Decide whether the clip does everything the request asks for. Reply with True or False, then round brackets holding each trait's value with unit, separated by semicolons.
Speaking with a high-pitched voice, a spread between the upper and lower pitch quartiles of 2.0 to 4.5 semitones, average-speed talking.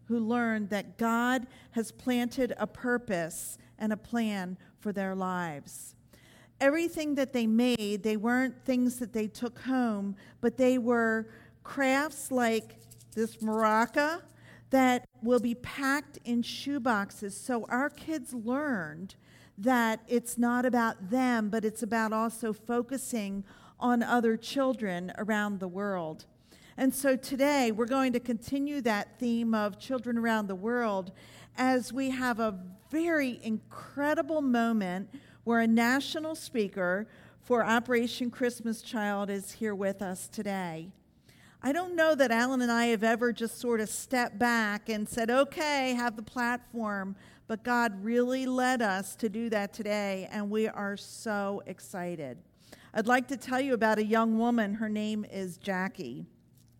True (230 Hz; 3.3 semitones; 145 wpm)